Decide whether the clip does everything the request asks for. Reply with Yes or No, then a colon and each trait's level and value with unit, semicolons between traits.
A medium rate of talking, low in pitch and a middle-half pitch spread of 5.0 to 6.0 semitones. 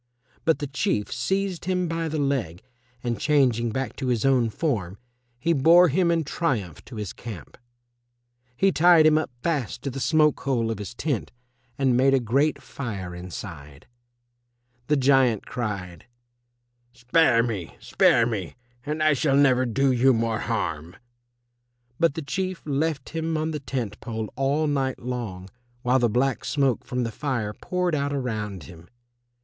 Yes: average, 160 wpm; low, 130 Hz; average, 5.3 semitones